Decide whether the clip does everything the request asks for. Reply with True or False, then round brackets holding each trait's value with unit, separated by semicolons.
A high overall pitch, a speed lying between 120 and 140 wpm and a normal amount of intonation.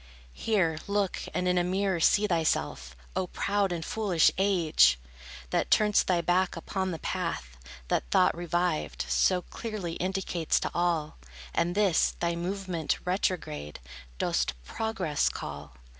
False (175 Hz; 135 wpm; 3.0 semitones)